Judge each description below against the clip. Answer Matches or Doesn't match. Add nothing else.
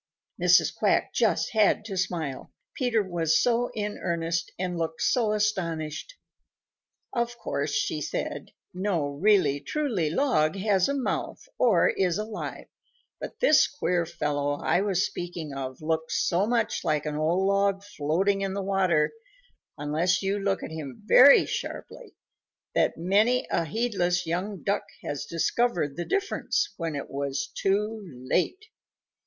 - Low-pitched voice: Doesn't match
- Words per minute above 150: Doesn't match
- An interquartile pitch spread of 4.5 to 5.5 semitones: Matches